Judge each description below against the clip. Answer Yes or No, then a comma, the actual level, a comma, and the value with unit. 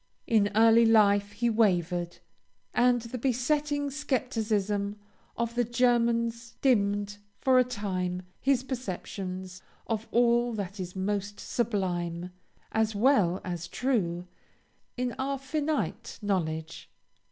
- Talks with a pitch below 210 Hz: No, high, 220 Hz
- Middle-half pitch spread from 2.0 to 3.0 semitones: No, average, 4.3 semitones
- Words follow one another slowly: Yes, slow, 110 wpm